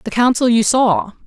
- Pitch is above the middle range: Yes, high, 235 Hz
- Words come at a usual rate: Yes, average, 190 wpm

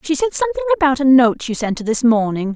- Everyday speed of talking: No, fast, 260 wpm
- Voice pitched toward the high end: Yes, very high, 270 Hz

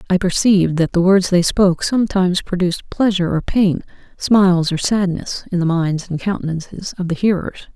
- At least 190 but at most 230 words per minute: No, average, 180 wpm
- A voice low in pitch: No, medium, 180 Hz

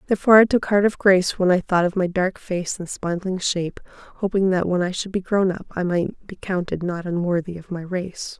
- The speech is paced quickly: Yes, fast, 235 wpm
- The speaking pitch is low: No, medium, 185 Hz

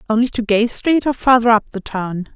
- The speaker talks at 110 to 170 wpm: No, fast, 230 wpm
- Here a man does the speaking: No, female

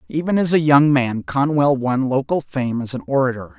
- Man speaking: Yes, male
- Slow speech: No, average, 200 wpm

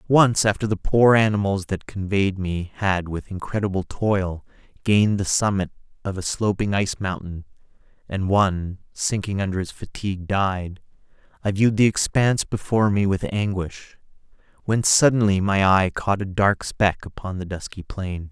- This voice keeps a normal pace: Yes, average, 155 wpm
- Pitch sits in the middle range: No, low, 100 Hz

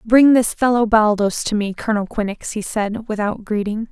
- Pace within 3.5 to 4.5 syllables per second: No, 5.0 syllables/s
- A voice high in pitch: Yes, high, 215 Hz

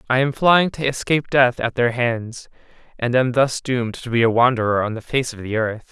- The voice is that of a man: Yes, male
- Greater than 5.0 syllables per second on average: Yes, 5.3 syllables/s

